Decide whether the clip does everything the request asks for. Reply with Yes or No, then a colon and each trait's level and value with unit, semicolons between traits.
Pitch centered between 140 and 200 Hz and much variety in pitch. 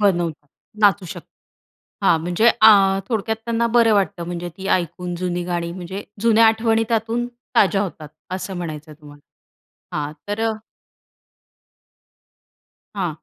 No: high, 190 Hz; average, 4.3 semitones